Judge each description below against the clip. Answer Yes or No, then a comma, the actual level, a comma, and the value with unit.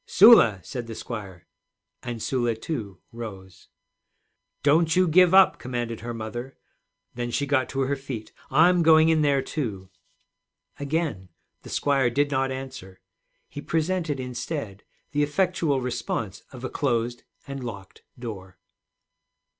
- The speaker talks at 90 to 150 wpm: Yes, slow, 135 wpm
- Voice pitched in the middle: No, low, 130 Hz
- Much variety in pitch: No, average, 4.4 semitones